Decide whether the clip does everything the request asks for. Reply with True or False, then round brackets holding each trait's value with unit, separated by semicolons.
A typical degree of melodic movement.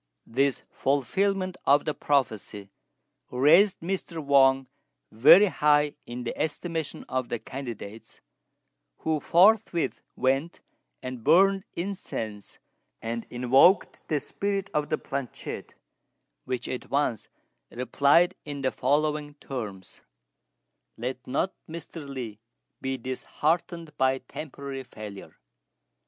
True (4.4 semitones)